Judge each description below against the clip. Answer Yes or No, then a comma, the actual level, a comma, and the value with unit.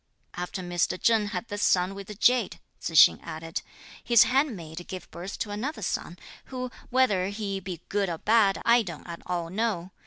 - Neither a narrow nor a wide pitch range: Yes, average, 4.2 semitones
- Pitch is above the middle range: Yes, high, 195 Hz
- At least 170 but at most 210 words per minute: Yes, average, 185 wpm